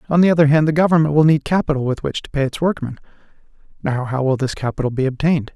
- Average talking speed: No, fast, 240 wpm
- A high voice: No, medium, 145 Hz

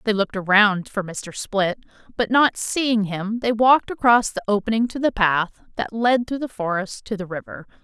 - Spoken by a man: No, female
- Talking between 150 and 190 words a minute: No, average, 200 wpm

